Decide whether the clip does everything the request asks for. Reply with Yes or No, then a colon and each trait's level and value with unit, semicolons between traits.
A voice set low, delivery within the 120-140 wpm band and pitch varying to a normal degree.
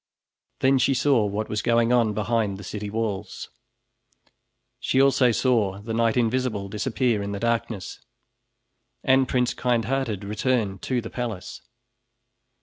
Yes: low, 115 Hz; slow, 135 wpm; average, 3.2 semitones